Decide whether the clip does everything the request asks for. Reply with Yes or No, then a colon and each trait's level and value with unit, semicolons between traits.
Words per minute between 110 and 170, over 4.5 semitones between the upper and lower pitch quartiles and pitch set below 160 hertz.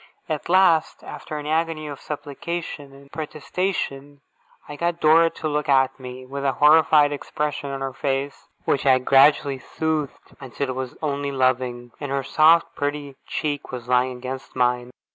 No: average, 160 wpm; narrow, 2.5 semitones; medium, 140 Hz